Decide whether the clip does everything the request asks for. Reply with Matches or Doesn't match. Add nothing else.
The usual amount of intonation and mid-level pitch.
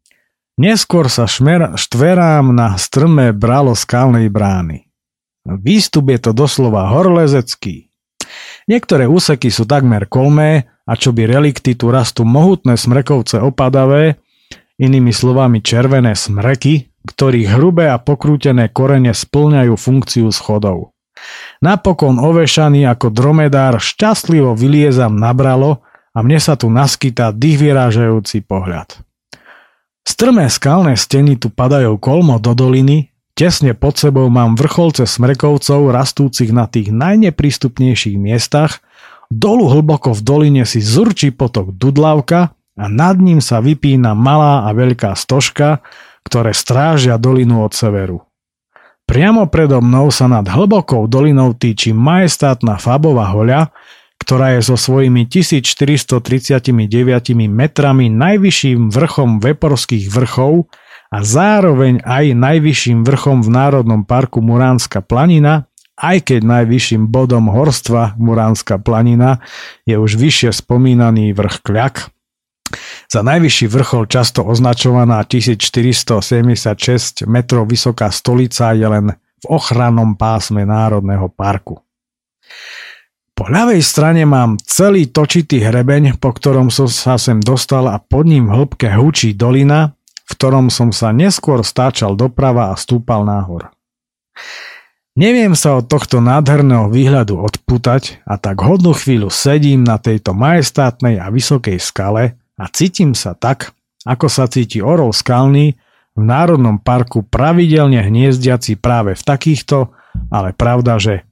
Doesn't match